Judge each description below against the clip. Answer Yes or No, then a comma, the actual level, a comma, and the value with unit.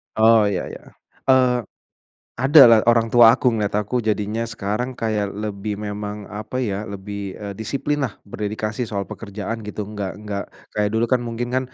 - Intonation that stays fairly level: Yes, narrow, 2.3 semitones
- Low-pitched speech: Yes, low, 105 Hz